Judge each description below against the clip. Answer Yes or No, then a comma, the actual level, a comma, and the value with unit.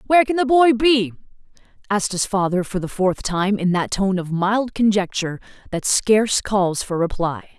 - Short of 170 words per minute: No, average, 180 wpm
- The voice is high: Yes, high, 205 Hz